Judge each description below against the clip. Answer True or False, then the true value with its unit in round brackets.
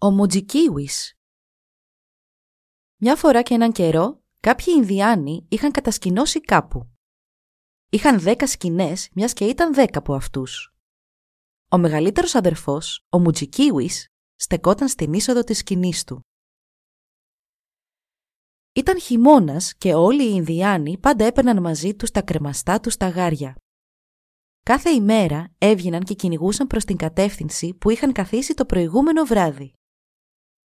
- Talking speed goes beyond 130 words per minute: False (120 wpm)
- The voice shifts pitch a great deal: True (7.0 semitones)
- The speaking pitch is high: True (200 Hz)